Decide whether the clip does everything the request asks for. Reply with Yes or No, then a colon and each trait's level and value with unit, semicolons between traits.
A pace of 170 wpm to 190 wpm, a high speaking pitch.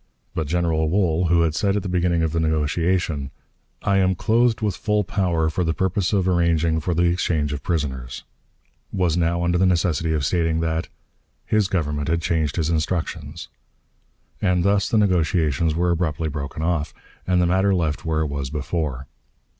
No: average, 180 wpm; very low, 85 Hz